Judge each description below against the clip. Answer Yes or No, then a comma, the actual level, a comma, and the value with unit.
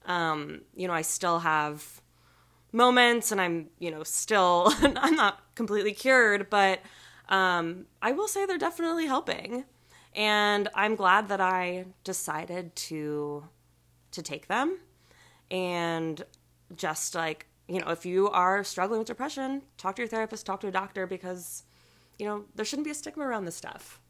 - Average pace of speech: Yes, average, 160 wpm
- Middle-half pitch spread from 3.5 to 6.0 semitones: Yes, average, 4.9 semitones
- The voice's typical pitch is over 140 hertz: Yes, medium, 185 Hz